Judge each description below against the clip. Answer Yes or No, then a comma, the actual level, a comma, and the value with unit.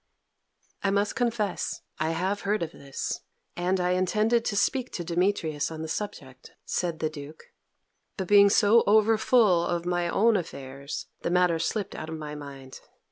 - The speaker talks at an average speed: Yes, average, 165 wpm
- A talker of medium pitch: Yes, medium, 180 Hz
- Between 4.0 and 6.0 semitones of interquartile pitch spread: Yes, average, 4.5 semitones